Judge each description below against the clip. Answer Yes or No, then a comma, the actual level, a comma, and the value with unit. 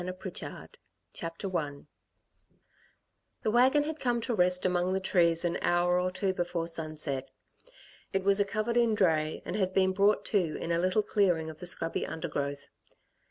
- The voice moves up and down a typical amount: Yes, average, 3.4 semitones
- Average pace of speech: Yes, average, 165 wpm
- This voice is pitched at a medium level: Yes, medium, 180 Hz